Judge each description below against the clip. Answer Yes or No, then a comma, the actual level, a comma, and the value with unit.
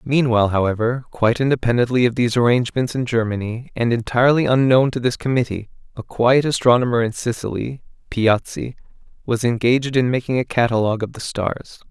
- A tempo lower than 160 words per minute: Yes, average, 150 wpm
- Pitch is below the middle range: Yes, low, 120 Hz